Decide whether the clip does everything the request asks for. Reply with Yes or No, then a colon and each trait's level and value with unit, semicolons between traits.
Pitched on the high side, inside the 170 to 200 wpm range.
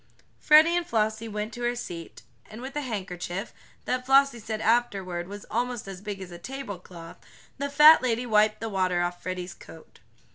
Yes: high, 215 Hz; average, 185 wpm